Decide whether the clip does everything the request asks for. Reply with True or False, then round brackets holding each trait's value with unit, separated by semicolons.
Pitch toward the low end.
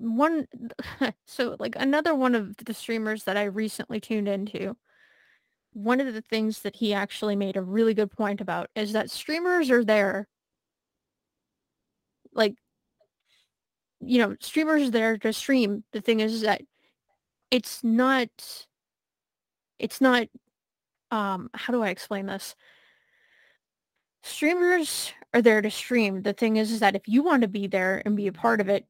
False (225 Hz)